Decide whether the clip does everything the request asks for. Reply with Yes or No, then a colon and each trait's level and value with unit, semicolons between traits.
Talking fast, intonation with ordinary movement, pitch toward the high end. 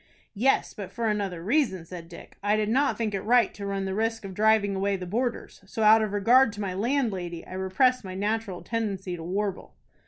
Yes: fast, 215 wpm; average, 3.0 semitones; high, 205 Hz